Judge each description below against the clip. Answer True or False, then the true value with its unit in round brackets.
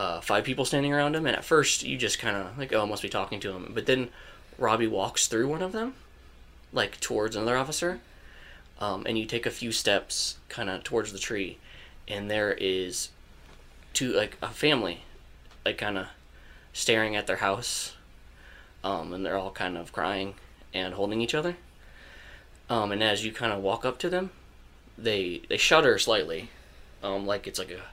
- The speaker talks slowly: False (190 wpm)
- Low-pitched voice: True (100 Hz)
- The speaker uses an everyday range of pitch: False (6.5 semitones)